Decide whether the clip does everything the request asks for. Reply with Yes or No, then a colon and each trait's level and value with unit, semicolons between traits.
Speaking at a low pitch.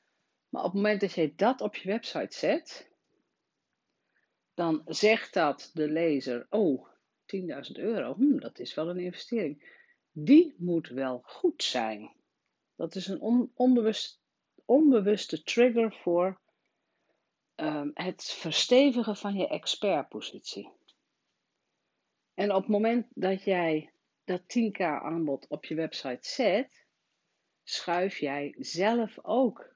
No: medium, 185 Hz